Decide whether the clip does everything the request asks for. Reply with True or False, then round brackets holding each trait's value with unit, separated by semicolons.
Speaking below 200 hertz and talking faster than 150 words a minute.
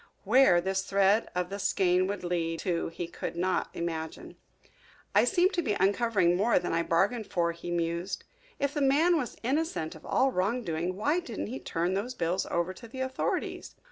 True (190 Hz; 190 wpm)